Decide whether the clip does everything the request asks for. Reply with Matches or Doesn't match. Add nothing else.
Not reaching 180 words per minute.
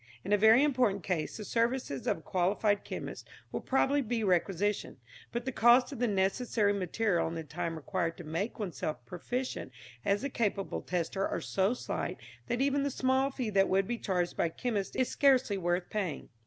Doesn't match